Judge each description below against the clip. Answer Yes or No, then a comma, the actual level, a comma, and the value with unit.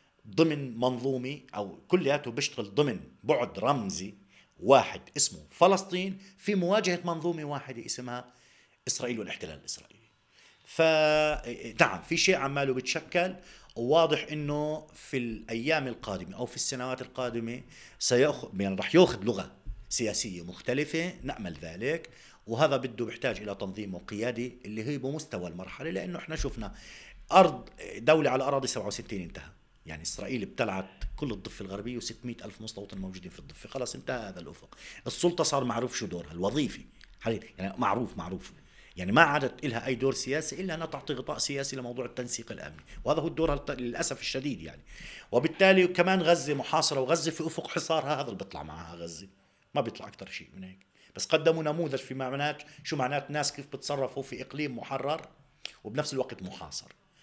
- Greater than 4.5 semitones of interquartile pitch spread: Yes, wide, 5.4 semitones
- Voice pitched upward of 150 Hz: No, low, 135 Hz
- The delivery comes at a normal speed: No, fast, 150 wpm